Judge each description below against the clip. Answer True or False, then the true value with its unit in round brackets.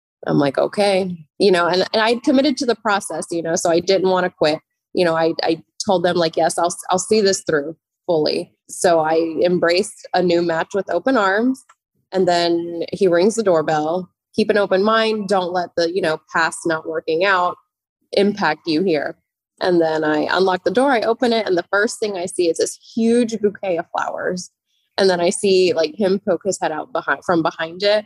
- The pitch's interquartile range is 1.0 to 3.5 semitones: True (3.2 semitones)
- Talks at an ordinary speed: False (215 wpm)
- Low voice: False (180 Hz)